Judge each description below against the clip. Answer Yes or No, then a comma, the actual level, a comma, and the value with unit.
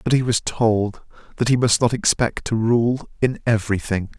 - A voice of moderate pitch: No, low, 115 Hz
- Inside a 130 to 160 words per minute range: No, average, 200 wpm